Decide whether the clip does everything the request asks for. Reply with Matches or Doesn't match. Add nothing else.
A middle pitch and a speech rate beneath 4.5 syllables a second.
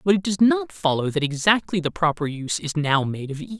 Doesn't match